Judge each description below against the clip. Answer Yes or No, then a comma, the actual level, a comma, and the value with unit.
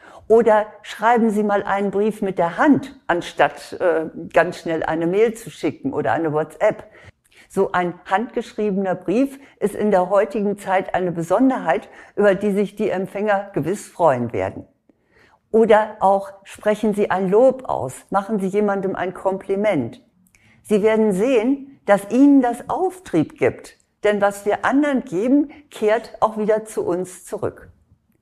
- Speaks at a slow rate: No, average, 150 wpm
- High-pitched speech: Yes, high, 205 Hz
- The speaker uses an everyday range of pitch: Yes, average, 3.0 semitones